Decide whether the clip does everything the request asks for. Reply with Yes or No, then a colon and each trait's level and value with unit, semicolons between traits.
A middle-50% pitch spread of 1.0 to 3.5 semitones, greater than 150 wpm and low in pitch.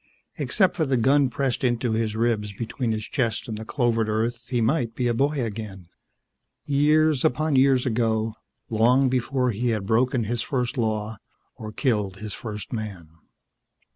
Yes: average, 3.1 semitones; average, 165 wpm; low, 120 Hz